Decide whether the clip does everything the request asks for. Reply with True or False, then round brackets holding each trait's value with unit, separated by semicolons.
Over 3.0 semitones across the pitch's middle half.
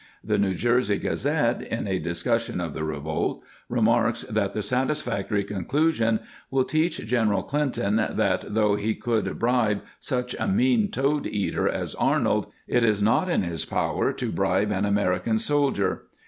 True (4.4 semitones)